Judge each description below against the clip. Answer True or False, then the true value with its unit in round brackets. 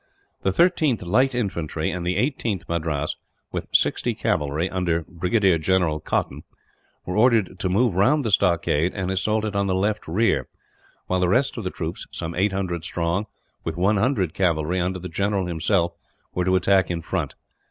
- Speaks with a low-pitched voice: True (95 Hz)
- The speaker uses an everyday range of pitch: True (3.5 semitones)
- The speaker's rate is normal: True (170 wpm)